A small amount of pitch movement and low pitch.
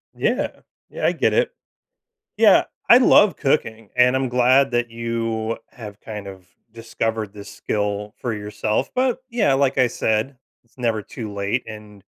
No: average, 3.4 semitones; low, 115 Hz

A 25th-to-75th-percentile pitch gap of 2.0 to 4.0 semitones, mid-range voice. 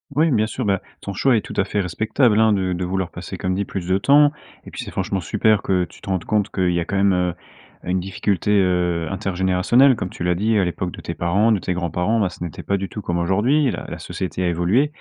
No: average, 3.2 semitones; very low, 95 Hz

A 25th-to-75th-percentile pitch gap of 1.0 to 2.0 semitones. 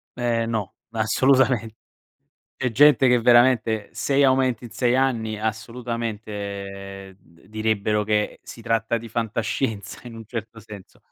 No: narrow, 2.4 semitones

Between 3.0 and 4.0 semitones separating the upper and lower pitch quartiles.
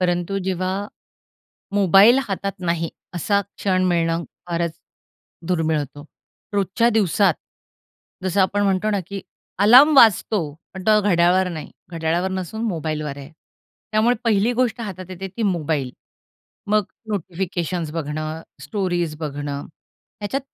Yes: average, 3.6 semitones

